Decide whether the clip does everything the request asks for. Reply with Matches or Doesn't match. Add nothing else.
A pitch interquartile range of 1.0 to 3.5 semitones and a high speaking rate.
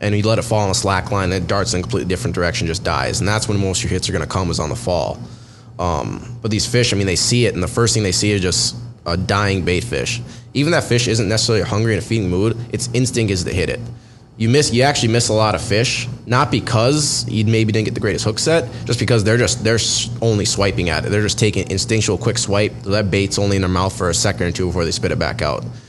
Matches